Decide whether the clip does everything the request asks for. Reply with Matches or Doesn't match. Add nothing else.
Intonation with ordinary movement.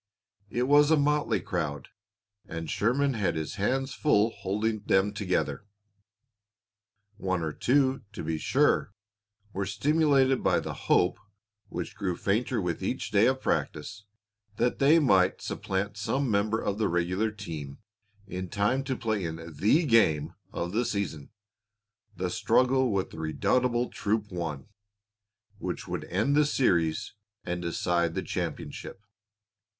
Doesn't match